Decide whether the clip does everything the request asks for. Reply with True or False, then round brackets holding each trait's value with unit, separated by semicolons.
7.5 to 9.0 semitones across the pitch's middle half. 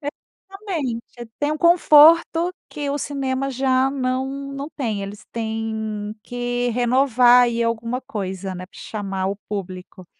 False (4.2 semitones)